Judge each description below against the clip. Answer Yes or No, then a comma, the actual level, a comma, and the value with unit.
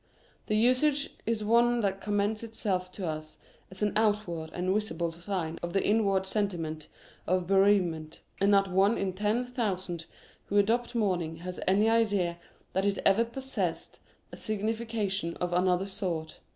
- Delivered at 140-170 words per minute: Yes, average, 150 wpm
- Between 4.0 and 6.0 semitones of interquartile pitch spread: No, average, 3.3 semitones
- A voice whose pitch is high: Yes, high, 195 Hz